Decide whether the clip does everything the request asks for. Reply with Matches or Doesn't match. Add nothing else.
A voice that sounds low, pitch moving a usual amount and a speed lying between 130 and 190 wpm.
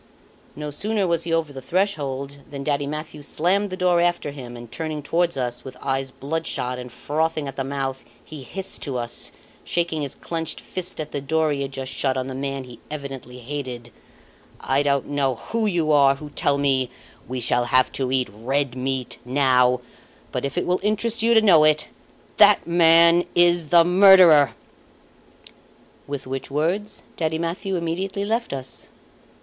Doesn't match